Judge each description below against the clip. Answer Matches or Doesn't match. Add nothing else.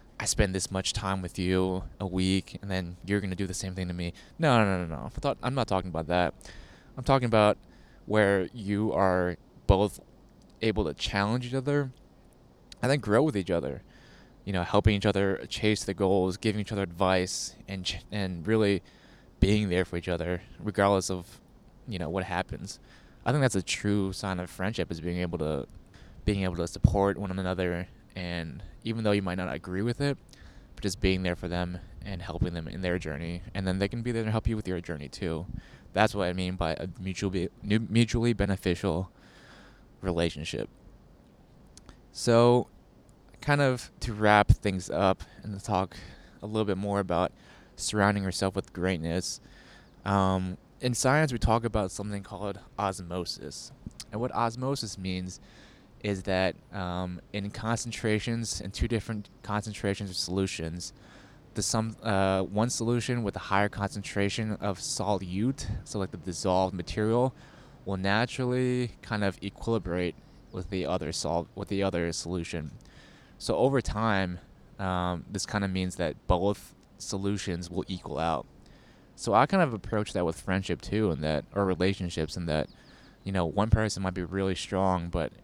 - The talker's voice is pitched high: Doesn't match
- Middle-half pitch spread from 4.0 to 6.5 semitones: Doesn't match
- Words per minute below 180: Matches